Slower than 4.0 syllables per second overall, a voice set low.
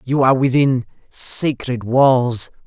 Yes: 3.6 syllables/s; low, 125 Hz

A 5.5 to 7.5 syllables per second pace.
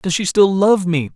No: 4.6 syllables/s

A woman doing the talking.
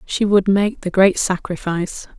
Yes: female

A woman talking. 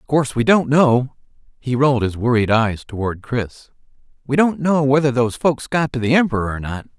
No: male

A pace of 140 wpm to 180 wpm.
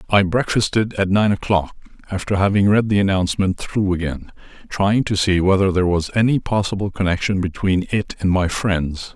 Yes: average, 170 wpm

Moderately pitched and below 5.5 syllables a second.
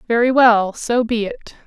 No: high, 240 Hz; 4.8 syllables/s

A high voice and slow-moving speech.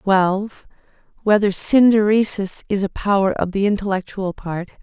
Yes: high, 200 Hz; slow, 125 wpm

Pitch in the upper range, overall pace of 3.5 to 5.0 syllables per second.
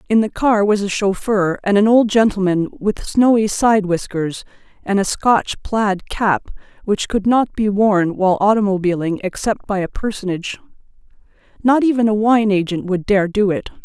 Yes: high, 205 Hz; 4.8 syllables/s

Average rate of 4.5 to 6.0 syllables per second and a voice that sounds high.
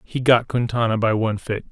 No: 5.8 syllables/s; low, 115 Hz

